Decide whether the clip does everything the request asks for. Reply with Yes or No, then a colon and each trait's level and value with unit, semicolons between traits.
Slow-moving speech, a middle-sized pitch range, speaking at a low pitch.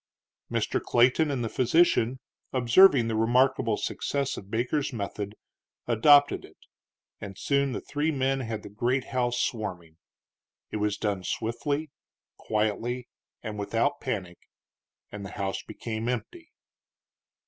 Yes: slow, 125 wpm; average, 4.2 semitones; low, 120 Hz